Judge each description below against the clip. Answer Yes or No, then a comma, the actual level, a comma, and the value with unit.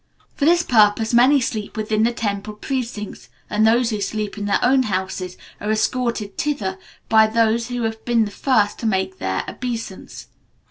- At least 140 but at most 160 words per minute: No, average, 175 wpm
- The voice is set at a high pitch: Yes, high, 220 Hz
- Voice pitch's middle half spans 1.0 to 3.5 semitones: Yes, narrow, 2.6 semitones